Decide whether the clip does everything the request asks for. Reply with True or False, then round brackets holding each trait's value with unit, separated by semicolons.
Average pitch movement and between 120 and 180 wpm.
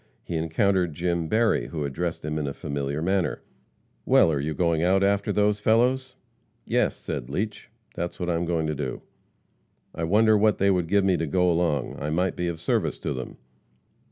False (4.1 semitones; 195 wpm)